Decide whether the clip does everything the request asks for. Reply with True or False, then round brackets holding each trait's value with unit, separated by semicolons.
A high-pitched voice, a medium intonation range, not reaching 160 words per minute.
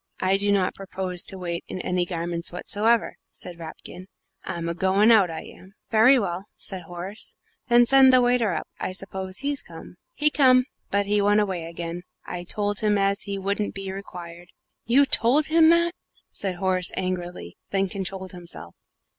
False (195 Hz; 3.5 semitones; 180 wpm)